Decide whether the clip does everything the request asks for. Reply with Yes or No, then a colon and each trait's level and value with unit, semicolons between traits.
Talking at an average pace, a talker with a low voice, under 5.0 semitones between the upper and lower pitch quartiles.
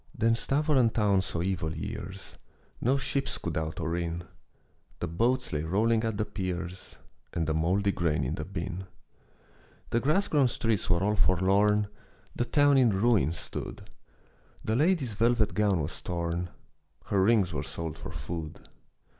No: average, 155 wpm; very low, 95 Hz; average, 5.3 semitones